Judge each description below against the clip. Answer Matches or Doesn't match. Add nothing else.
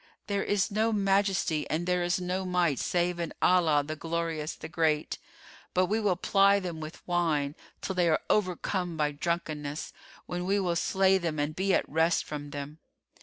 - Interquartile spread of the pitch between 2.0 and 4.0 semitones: Matches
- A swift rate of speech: Doesn't match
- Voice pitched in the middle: Matches